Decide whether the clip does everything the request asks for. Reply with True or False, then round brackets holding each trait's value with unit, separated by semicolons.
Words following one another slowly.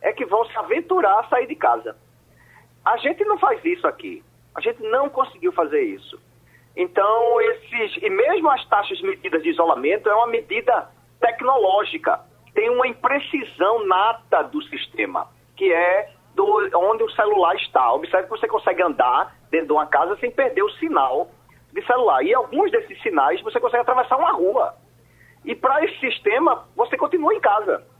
False (170 wpm)